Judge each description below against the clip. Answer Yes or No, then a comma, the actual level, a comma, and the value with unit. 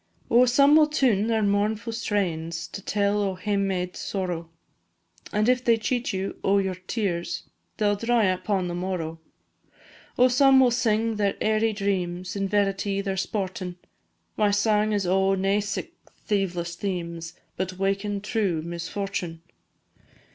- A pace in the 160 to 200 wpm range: No, average, 145 wpm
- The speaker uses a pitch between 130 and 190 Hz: No, high, 200 Hz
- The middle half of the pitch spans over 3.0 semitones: No, average, 2.7 semitones